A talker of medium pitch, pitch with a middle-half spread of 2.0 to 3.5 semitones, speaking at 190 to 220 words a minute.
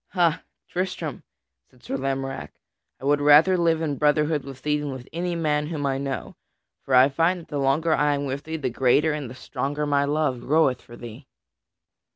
Yes: medium, 145 Hz; average, 2.8 semitones; average, 195 wpm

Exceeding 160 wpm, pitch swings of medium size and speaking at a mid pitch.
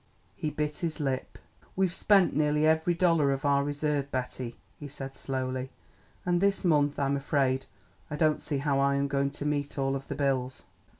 No: average, 185 wpm; narrow, 2.0 semitones; medium, 145 Hz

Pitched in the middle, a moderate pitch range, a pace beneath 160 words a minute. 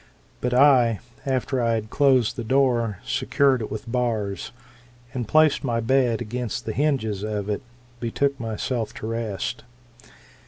No: low, 120 Hz; average, 3.1 semitones; average, 145 wpm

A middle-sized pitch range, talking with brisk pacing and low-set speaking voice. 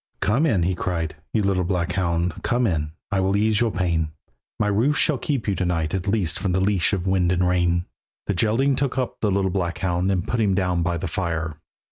Yes: average, 3.2 semitones; fast, 230 wpm; very low, 95 Hz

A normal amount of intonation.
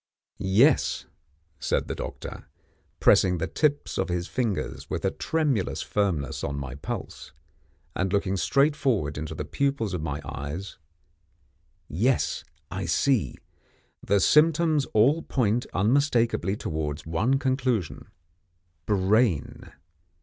No: wide, 8.0 semitones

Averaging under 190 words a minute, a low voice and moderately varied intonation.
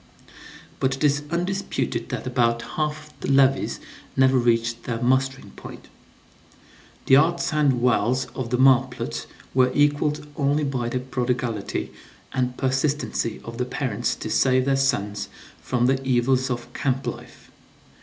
No: average, 140 wpm; low, 130 Hz; narrow, 2.1 semitones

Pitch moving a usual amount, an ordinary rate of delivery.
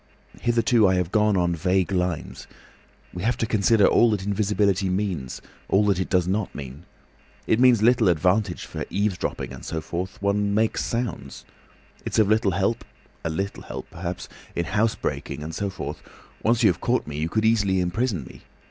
Yes: average, 3.5 semitones; average, 165 wpm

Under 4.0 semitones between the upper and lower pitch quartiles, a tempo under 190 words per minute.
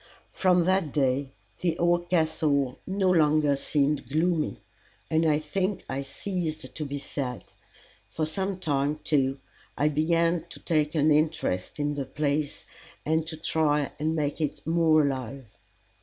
Yes: narrow, 2.6 semitones; average, 145 wpm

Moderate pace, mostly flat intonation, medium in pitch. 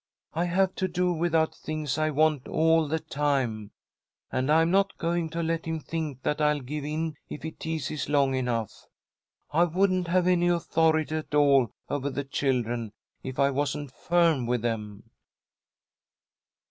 No: average, 160 wpm; average, 3.4 semitones; medium, 155 Hz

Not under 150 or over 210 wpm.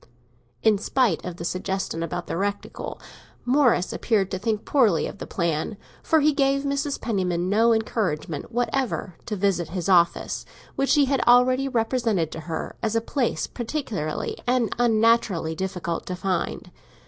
Yes: average, 155 wpm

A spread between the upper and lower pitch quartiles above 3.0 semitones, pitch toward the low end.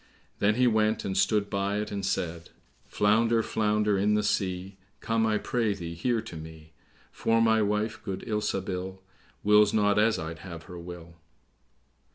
No: average, 2.7 semitones; low, 105 Hz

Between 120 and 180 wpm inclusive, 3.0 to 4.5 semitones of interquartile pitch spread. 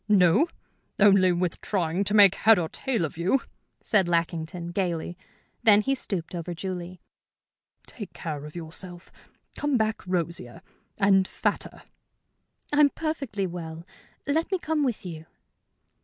Yes: slow, 135 wpm; average, 4.2 semitones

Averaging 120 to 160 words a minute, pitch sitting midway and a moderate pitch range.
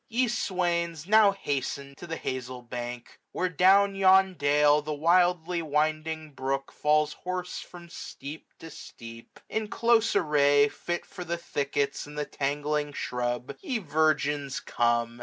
Yes: average, 140 wpm; medium, 155 Hz; average, 4.3 semitones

